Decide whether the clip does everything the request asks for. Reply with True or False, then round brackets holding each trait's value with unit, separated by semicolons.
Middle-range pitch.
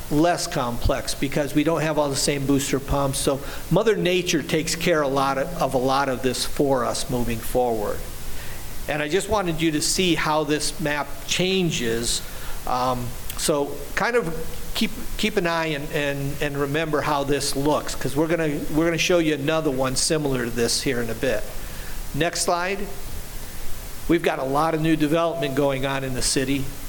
True (145 Hz)